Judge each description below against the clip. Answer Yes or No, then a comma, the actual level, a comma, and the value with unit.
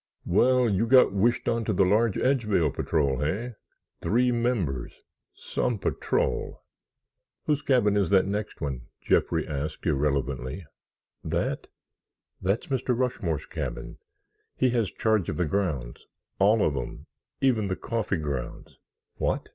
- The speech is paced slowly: Yes, slow, 125 wpm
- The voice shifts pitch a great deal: Yes, wide, 7.4 semitones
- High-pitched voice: No, low, 100 Hz